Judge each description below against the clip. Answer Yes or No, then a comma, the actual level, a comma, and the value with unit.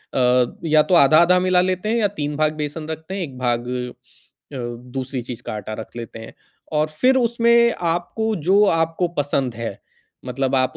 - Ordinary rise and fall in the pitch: No, wide, 6.4 semitones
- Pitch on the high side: No, medium, 155 Hz